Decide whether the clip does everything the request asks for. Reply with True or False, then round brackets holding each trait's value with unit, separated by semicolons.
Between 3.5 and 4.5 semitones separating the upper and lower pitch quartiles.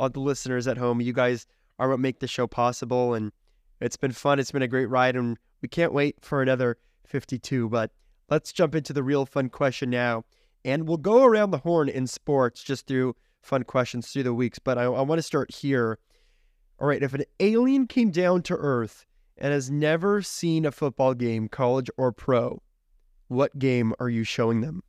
False (2.8 semitones)